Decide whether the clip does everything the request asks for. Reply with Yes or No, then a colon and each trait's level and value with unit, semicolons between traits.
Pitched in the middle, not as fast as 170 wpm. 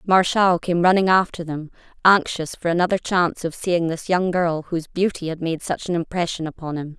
No: medium, 175 Hz; average, 200 wpm